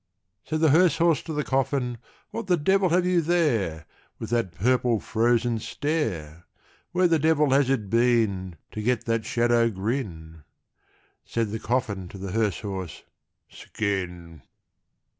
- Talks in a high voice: No, low, 120 Hz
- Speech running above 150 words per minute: No, average, 145 wpm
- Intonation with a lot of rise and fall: Yes, wide, 7.0 semitones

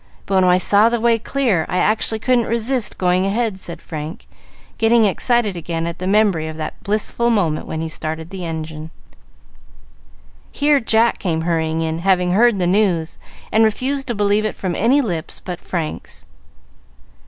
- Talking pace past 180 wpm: No, average, 170 wpm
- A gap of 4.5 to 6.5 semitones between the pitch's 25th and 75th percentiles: Yes, wide, 5.4 semitones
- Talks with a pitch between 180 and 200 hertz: Yes, high, 190 Hz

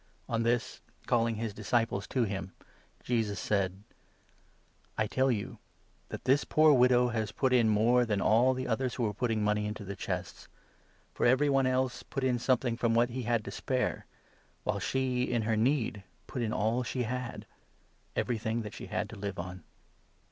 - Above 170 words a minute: Yes, average, 190 wpm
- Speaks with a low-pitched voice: Yes, low, 115 Hz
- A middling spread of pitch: Yes, average, 3.1 semitones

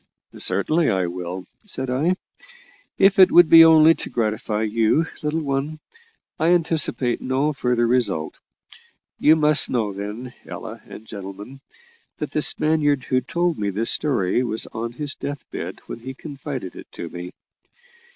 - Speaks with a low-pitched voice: Yes, low, 130 Hz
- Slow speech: No, average, 150 wpm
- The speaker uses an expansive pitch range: Yes, wide, 6.0 semitones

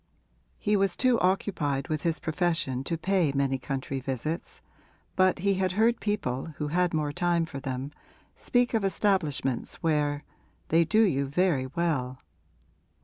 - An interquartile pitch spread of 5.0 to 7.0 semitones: Yes, average, 5.3 semitones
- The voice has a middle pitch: Yes, medium, 165 Hz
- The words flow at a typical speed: Yes, average, 145 wpm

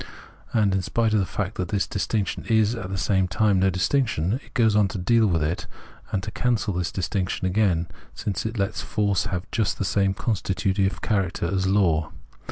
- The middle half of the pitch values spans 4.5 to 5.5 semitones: No, narrow, 2.6 semitones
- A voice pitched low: Yes, low, 100 Hz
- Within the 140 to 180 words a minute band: No, average, 195 wpm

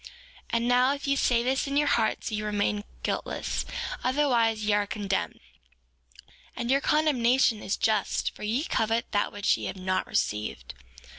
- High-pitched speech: Yes, high, 230 Hz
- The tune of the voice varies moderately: Yes, average, 4.0 semitones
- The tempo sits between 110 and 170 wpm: Yes, average, 165 wpm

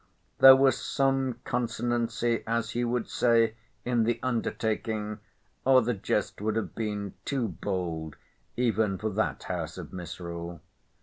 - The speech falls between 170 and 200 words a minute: No, slow, 135 wpm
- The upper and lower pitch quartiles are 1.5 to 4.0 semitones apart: Yes, average, 3.7 semitones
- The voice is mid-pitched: No, low, 110 Hz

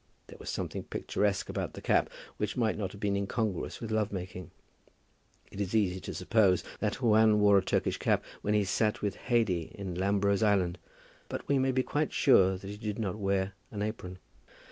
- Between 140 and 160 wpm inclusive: No, average, 195 wpm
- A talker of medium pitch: No, low, 100 Hz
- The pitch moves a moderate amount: No, narrow, 2.3 semitones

